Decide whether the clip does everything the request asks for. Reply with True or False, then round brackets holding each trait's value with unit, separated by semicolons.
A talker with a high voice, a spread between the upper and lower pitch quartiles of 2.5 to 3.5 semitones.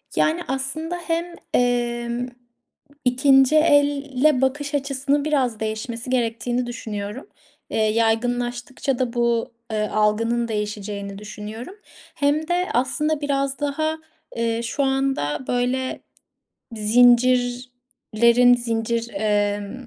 True (245 Hz; 3.2 semitones)